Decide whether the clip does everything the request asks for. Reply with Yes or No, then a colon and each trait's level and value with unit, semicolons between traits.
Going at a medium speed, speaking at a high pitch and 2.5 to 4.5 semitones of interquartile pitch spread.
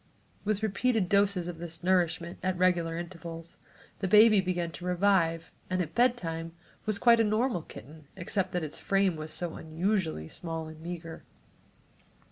No: average, 155 wpm; medium, 175 Hz; average, 3.2 semitones